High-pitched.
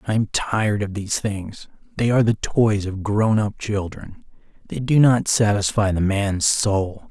No: low, 105 Hz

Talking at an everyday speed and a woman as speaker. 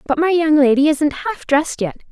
No: fast, 225 wpm; female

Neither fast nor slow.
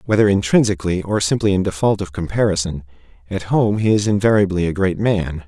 Yes: average, 175 wpm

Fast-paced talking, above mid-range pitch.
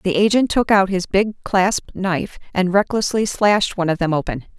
No: average, 195 wpm; high, 195 Hz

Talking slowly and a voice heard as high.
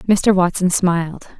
No: slow, 130 wpm; medium, 180 Hz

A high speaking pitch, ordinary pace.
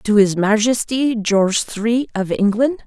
Yes: high, 220 Hz; average, 145 wpm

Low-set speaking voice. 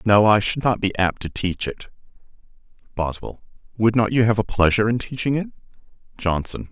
Yes: low, 105 Hz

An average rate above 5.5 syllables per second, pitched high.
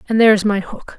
Yes: 7.4 syllables/s; high, 210 Hz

